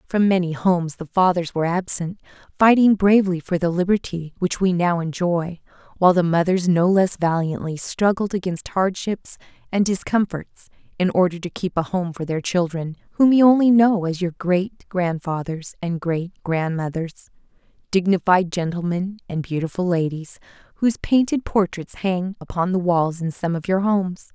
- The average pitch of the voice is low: No, medium, 180 Hz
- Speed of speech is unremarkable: Yes, average, 160 wpm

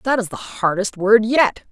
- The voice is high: Yes, high, 220 Hz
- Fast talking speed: Yes, fast, 210 wpm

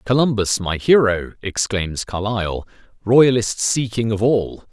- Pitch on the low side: Yes, low, 110 Hz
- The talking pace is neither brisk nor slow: No, slow, 125 wpm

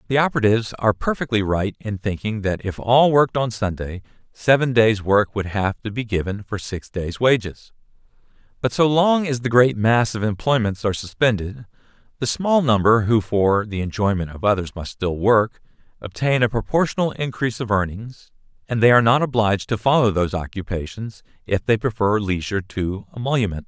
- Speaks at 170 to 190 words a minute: Yes, average, 175 wpm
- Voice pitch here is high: No, low, 110 Hz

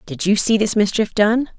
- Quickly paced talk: Yes, fast, 230 wpm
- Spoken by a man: No, female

